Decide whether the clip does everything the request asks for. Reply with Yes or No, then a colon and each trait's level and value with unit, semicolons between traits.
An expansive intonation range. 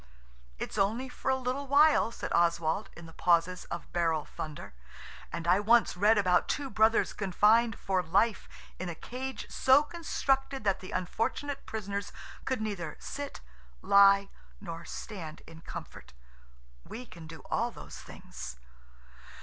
Yes: wide, 6.3 semitones